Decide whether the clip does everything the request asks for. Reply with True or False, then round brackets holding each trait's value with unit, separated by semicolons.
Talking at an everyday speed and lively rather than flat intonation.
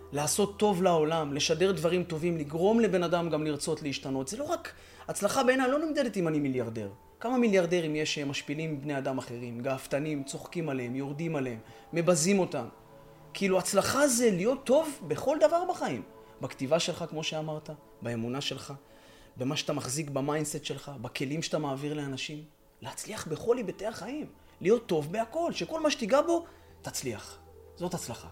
False (155 wpm; 6.2 semitones)